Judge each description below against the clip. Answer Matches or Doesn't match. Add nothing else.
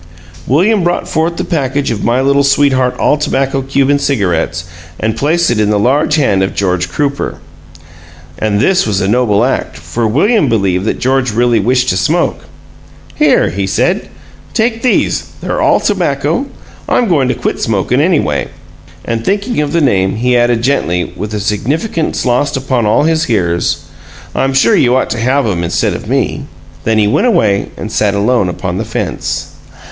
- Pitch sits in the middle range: Doesn't match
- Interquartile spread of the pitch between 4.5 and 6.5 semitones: Matches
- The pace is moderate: Matches